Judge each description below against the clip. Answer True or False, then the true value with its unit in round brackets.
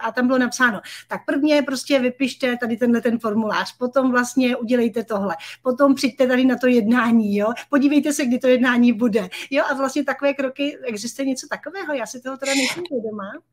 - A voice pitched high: True (255 Hz)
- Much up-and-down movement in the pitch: False (2.6 semitones)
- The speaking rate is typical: False (190 wpm)